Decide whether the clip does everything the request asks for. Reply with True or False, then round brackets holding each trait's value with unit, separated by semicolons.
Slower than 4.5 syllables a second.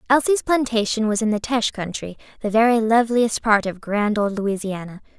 False (5.4 syllables/s)